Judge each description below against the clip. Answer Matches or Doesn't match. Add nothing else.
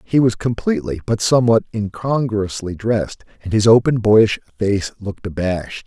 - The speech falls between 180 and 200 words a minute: Doesn't match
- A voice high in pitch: Doesn't match